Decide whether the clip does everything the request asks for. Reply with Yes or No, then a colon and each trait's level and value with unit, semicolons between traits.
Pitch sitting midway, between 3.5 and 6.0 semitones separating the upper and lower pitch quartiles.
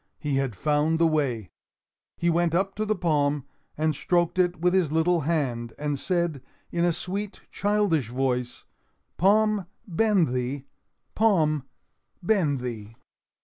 Yes: medium, 160 Hz; average, 4.7 semitones